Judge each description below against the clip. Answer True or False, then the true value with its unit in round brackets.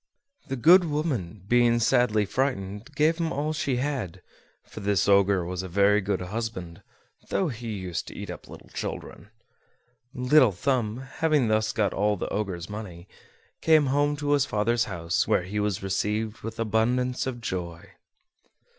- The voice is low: True (110 Hz)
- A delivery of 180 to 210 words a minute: False (160 wpm)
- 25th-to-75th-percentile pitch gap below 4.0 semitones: False (5.1 semitones)